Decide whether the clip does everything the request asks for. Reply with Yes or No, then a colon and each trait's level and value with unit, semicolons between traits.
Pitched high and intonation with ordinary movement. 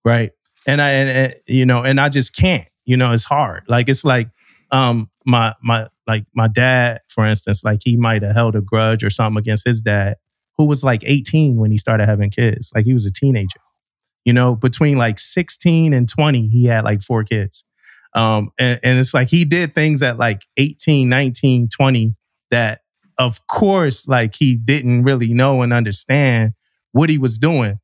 No: low, 120 Hz; average, 3.4 semitones